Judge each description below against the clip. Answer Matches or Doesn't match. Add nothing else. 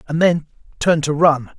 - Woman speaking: Doesn't match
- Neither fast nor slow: Matches